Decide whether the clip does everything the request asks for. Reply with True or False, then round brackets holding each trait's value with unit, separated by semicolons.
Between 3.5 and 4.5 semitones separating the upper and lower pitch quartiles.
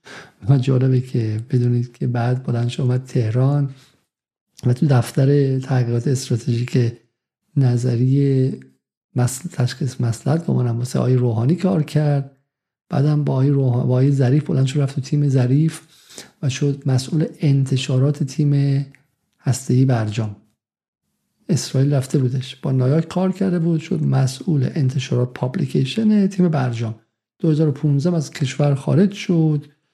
False (3.1 semitones)